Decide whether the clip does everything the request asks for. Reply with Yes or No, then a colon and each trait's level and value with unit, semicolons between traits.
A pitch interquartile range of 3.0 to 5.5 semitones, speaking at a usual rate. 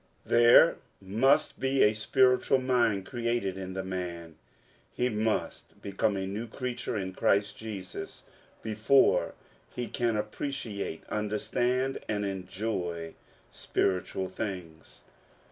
No: average, 4.1 semitones; slow, 110 wpm